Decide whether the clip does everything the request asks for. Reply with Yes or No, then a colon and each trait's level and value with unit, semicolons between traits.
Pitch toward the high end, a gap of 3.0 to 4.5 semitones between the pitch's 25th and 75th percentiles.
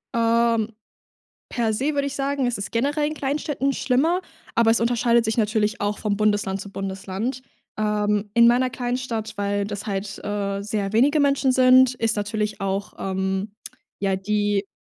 Yes: high, 220 Hz; average, 3.7 semitones